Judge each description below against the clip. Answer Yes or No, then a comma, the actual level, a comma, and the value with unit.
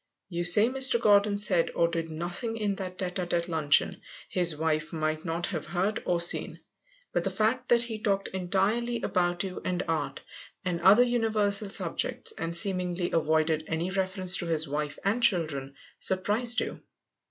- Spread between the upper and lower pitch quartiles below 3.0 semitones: No, average, 4.0 semitones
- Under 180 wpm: Yes, average, 170 wpm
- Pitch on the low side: No, medium, 185 Hz